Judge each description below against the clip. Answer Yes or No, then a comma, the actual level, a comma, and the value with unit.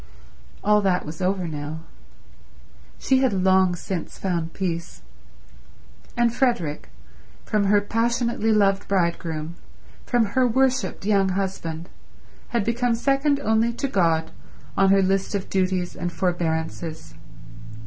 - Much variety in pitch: No, average, 4.9 semitones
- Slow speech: Yes, slow, 120 wpm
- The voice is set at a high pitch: Yes, high, 195 Hz